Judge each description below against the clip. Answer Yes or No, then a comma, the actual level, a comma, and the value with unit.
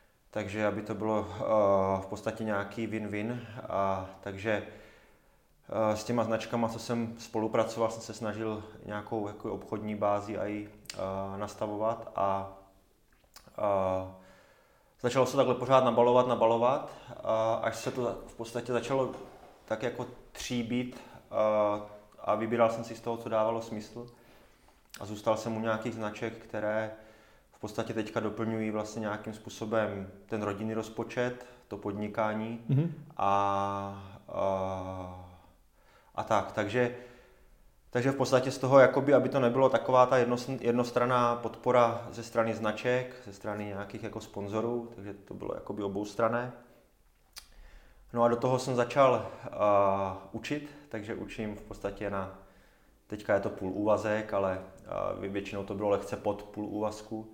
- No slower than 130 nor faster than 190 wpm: Yes, average, 140 wpm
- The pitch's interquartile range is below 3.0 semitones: Yes, narrow, 2.4 semitones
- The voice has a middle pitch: No, low, 110 Hz